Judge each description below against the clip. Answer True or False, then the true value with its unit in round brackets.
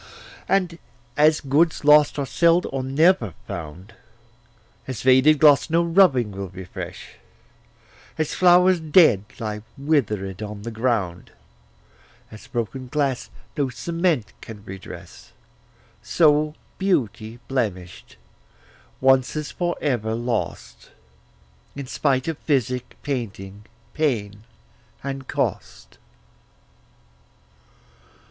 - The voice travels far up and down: True (6.2 semitones)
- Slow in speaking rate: True (100 wpm)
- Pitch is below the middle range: True (130 Hz)